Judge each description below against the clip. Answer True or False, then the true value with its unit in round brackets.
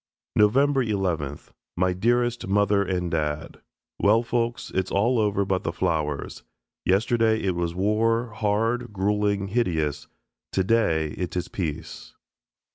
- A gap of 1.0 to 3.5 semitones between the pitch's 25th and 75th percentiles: False (4.3 semitones)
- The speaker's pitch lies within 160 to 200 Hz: False (100 Hz)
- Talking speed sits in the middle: False (120 wpm)